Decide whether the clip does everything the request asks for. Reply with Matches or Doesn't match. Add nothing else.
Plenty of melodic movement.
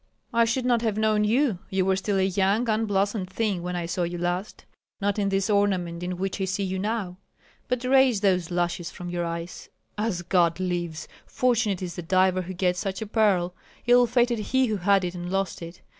Doesn't match